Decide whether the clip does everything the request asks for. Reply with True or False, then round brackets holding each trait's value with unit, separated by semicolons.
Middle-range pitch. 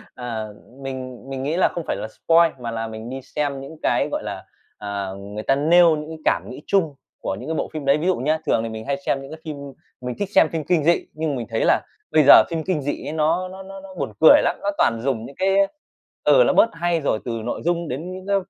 True (150 Hz)